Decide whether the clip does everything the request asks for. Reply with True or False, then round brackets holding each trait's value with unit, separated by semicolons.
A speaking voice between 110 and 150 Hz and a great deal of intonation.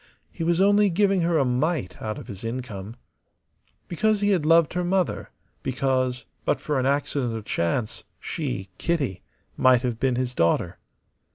True (135 Hz; 6.4 semitones)